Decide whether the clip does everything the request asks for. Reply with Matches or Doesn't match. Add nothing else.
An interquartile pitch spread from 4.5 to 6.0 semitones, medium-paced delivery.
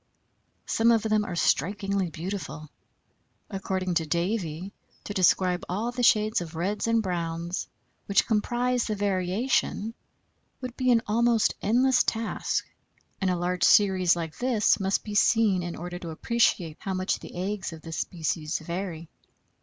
Doesn't match